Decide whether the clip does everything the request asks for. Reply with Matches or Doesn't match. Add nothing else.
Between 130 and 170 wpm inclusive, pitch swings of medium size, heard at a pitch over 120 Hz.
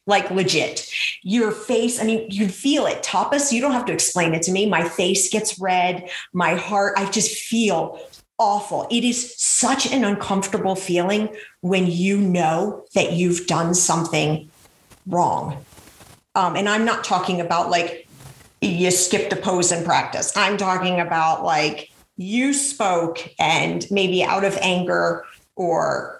Matches